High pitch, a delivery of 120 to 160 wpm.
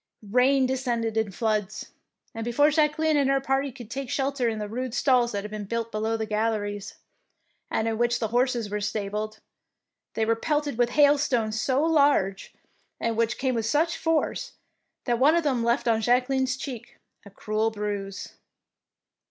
No: high, 235 Hz; average, 175 wpm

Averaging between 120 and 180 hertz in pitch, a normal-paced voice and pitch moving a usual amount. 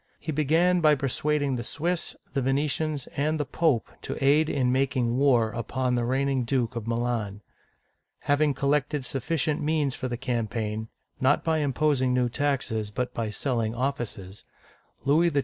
Yes: low, 135 Hz; average, 165 wpm; average, 3.5 semitones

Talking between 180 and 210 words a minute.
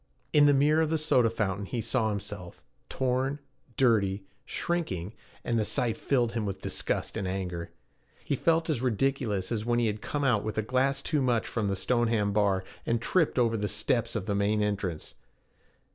Yes: average, 190 wpm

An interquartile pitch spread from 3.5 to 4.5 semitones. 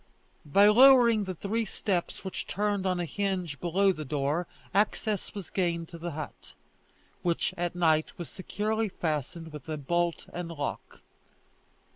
Yes: average, 3.8 semitones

